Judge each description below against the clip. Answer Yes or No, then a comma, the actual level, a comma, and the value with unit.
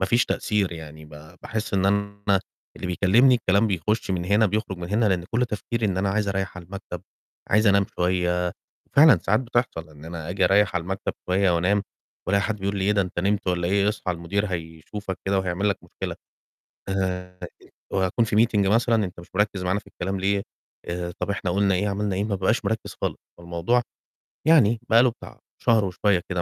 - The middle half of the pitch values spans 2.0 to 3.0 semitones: Yes, narrow, 2.6 semitones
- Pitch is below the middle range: Yes, very low, 95 Hz